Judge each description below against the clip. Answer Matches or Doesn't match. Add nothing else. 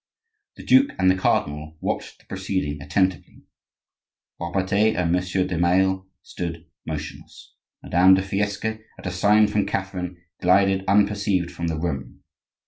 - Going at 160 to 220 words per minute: Doesn't match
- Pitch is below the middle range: Matches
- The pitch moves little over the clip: Matches